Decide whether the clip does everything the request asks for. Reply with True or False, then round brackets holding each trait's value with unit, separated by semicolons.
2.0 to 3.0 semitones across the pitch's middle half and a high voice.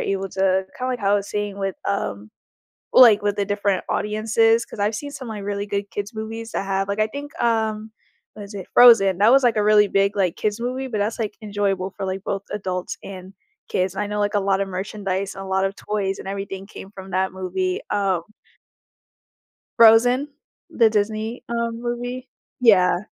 True (2.4 semitones; 205 Hz)